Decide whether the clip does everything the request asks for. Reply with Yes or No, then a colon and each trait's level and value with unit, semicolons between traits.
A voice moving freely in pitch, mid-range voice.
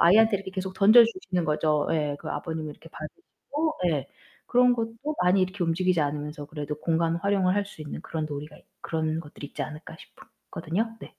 No: average, 4.6 semitones; medium, 165 Hz